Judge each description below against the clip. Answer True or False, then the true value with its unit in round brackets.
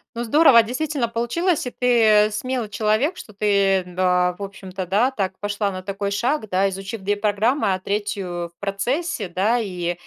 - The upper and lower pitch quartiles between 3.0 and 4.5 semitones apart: True (3.6 semitones)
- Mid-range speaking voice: False (205 Hz)